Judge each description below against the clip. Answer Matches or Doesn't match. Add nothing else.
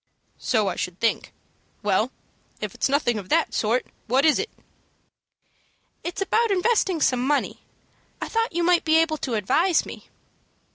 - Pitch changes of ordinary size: Doesn't match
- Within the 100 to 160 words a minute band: Matches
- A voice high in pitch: Matches